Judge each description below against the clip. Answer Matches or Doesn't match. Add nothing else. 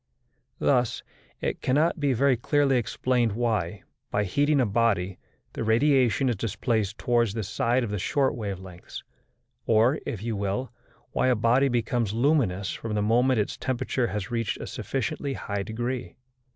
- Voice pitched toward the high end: Doesn't match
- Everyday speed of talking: Matches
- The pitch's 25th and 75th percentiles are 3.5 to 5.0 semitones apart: Matches